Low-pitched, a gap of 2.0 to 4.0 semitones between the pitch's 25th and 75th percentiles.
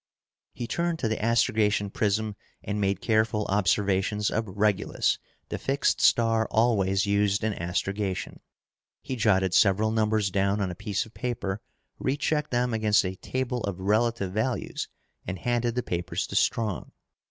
Yes: low, 105 Hz; average, 2.8 semitones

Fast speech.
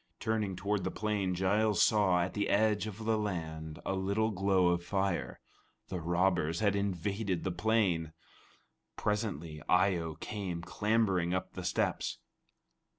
No: average, 145 wpm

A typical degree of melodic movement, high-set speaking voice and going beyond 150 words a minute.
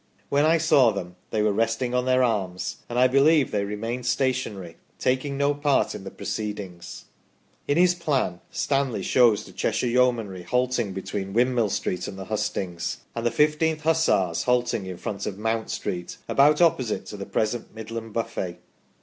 No: average, 4.5 semitones; low, 115 Hz; average, 170 wpm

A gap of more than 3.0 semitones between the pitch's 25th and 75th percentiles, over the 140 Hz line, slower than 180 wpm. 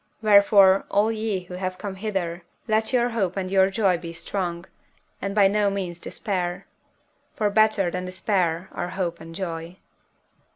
No: narrow, 2.6 semitones; high, 190 Hz; average, 160 wpm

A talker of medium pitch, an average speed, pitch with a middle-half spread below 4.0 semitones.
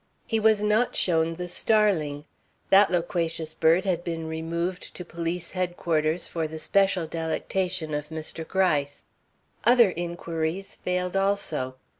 No: medium, 170 Hz; slow, 130 wpm; average, 2.9 semitones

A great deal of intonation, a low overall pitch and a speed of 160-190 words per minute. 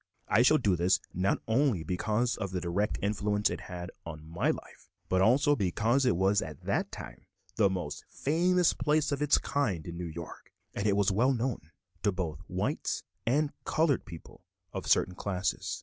Yes: wide, 6.3 semitones; low, 100 Hz; average, 180 wpm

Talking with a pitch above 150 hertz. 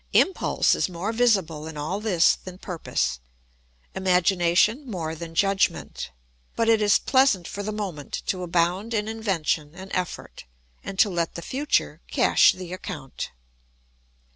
Yes: medium, 185 Hz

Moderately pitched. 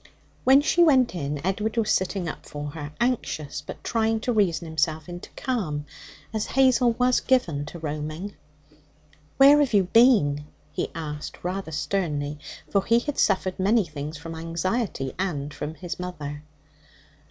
Yes: medium, 180 Hz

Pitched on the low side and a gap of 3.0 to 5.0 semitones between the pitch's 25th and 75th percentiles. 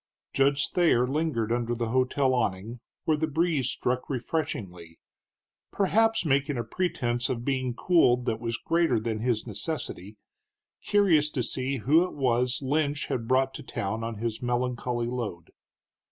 Yes: low, 125 Hz; average, 3.9 semitones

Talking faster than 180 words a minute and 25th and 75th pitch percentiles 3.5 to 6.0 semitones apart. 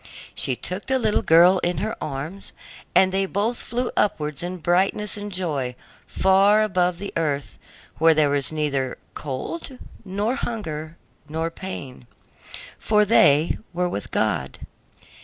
No: average, 140 wpm; average, 5.2 semitones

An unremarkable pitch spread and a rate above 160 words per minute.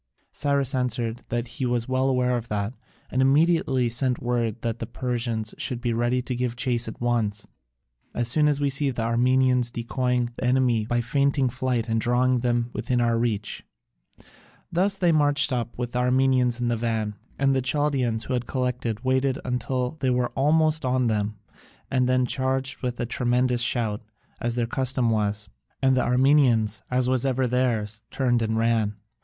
No: narrow, 1.9 semitones; average, 180 wpm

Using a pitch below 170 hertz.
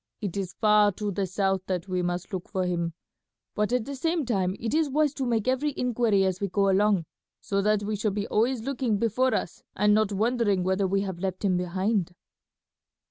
No: high, 205 Hz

